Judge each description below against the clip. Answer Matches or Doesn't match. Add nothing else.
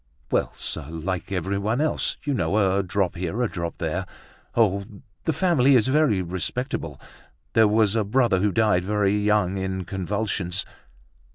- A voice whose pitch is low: Matches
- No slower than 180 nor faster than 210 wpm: Doesn't match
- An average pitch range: Matches